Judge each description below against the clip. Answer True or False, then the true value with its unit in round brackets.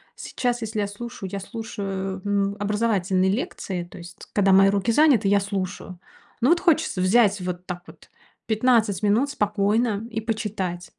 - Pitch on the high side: True (205 Hz)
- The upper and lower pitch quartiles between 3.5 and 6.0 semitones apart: False (2.9 semitones)